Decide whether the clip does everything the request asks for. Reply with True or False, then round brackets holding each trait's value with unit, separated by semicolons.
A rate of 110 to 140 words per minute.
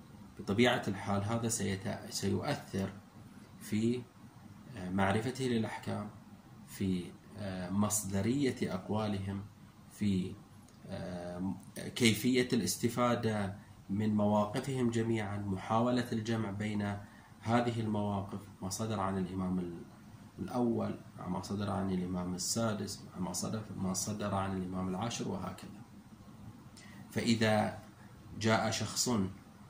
False (85 wpm)